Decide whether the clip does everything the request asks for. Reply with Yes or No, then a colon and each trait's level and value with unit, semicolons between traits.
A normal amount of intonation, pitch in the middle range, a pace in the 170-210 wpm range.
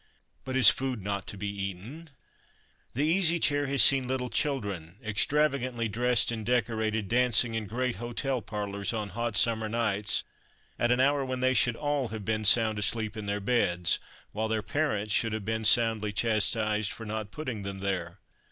No: average, 3.4 semitones; low, 110 Hz; average, 175 wpm